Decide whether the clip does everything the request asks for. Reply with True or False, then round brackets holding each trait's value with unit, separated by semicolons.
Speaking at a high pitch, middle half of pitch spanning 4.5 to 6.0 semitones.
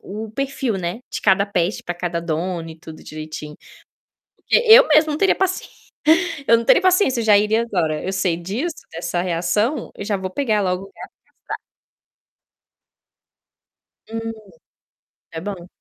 True (195 Hz; 5.1 semitones)